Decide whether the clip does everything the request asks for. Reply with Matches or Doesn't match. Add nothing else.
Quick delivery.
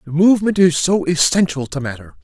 Doesn't match